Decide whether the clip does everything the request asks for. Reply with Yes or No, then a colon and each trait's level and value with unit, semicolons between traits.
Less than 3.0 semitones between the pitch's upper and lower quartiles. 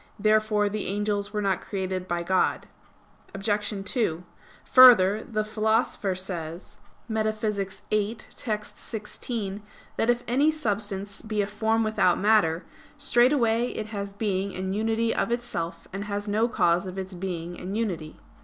Yes: narrow, 2.6 semitones